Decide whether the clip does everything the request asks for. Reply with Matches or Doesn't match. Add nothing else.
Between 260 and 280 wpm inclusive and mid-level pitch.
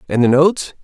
Doesn't match